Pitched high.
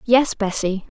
Yes: high, 215 Hz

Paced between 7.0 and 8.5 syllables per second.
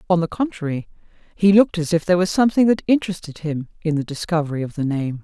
Yes: 7.1 syllables/s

